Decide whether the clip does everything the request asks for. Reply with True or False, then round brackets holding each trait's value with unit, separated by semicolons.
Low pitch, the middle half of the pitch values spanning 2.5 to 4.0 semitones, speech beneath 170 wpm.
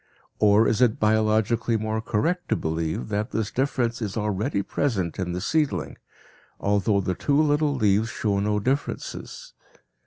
True (110 Hz; 3.5 semitones; 150 wpm)